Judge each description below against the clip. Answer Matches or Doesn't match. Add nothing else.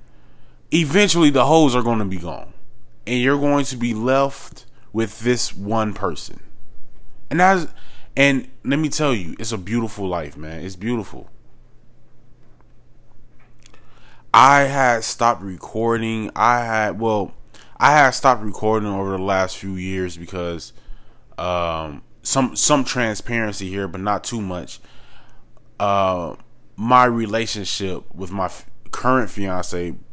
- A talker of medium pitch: Doesn't match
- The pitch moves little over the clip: Doesn't match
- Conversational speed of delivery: Doesn't match